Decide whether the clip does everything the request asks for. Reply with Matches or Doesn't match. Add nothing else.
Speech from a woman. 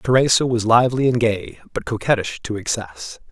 Doesn't match